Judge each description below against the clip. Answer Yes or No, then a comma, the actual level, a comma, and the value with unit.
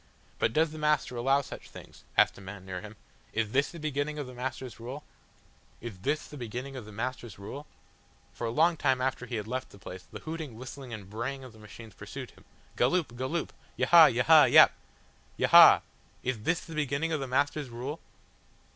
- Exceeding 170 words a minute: Yes, average, 200 wpm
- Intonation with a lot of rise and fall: No, average, 4.2 semitones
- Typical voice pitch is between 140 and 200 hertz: No, low, 130 Hz